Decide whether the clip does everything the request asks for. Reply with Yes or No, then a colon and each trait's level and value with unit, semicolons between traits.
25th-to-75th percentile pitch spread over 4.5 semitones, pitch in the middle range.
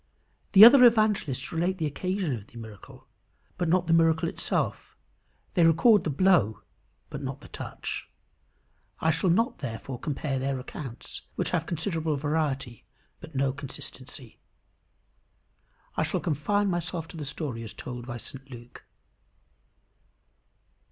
Yes: average, 5.0 semitones; medium, 155 Hz